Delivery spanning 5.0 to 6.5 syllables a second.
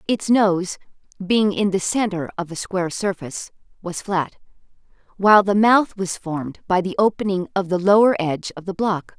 Yes: 5.1 syllables/s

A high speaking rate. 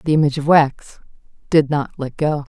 No: average, 190 wpm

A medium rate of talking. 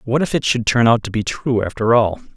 No: fast, 280 wpm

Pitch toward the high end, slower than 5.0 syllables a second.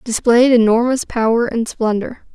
Yes: high, 235 Hz; 4.6 syllables/s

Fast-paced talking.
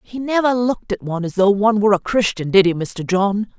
Yes: fast, 250 wpm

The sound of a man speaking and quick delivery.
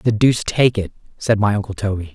Yes: male; fast, 225 wpm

